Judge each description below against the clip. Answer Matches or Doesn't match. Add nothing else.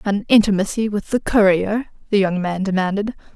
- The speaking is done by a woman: Matches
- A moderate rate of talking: Matches